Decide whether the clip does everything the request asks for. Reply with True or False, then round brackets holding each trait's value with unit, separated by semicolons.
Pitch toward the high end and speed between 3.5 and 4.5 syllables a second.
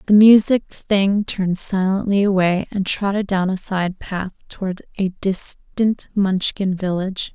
True (195 Hz; 4.1 syllables/s)